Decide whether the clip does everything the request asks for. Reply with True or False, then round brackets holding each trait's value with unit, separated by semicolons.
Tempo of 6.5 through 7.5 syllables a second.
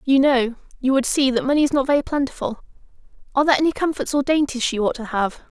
True (6.8 syllables/s)